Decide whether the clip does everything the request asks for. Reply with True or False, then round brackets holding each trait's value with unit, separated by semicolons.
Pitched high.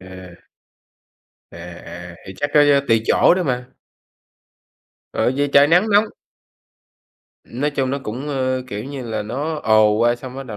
False (125 Hz)